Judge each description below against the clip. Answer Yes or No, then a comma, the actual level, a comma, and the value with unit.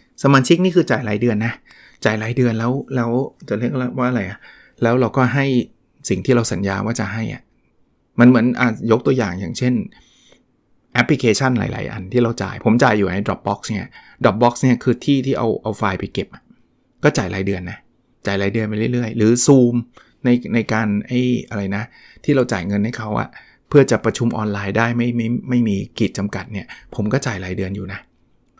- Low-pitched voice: Yes, low, 115 Hz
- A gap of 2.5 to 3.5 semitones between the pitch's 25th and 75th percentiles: Yes, average, 3.0 semitones